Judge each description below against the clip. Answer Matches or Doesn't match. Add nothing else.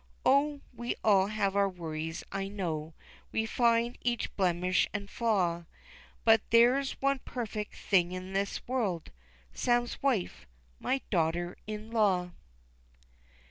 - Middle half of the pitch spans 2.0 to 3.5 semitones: Doesn't match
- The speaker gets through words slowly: Matches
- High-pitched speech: Matches